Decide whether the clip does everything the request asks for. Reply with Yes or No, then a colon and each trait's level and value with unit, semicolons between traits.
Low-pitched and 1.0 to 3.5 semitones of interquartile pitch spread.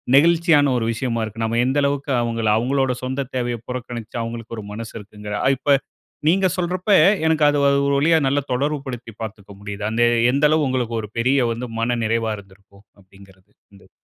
No: low, 120 Hz; average, 4.1 semitones